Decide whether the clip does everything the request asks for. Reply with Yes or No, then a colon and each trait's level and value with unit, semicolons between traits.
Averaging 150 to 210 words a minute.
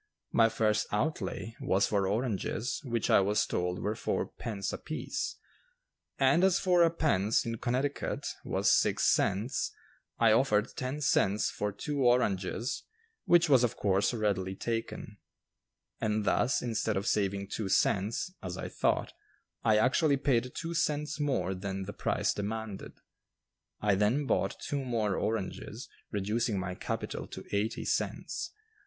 No: average, 140 wpm